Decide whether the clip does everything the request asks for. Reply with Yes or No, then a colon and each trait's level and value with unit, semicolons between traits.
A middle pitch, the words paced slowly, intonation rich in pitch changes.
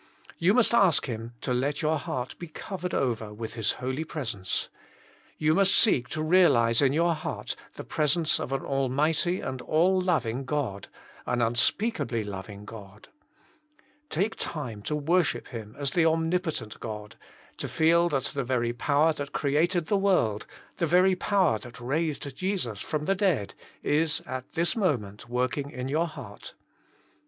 No: medium, 145 Hz; average, 165 wpm; wide, 6.0 semitones